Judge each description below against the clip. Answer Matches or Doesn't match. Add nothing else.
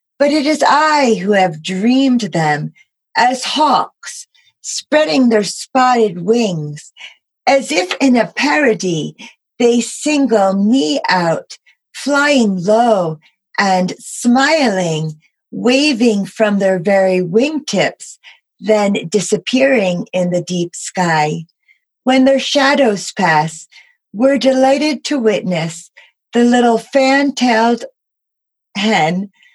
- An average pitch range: Doesn't match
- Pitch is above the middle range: Matches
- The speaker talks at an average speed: Doesn't match